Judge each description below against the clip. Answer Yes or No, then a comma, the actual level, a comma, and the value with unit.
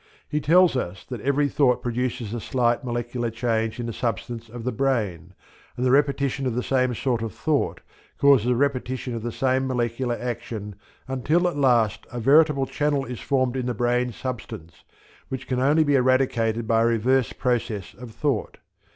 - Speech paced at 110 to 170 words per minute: No, average, 180 wpm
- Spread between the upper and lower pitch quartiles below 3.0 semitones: Yes, narrow, 2.5 semitones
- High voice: No, low, 125 Hz